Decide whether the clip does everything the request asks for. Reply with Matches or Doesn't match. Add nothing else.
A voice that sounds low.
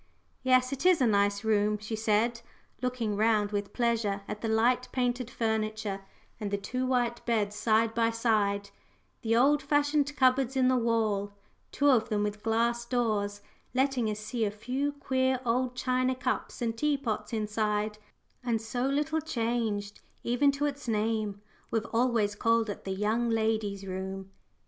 Doesn't match